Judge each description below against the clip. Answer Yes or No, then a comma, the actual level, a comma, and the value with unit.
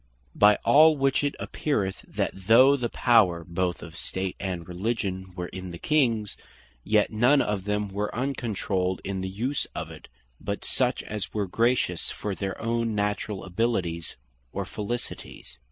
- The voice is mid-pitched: No, low, 105 Hz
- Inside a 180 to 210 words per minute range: No, average, 155 wpm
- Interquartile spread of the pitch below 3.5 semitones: No, average, 4.0 semitones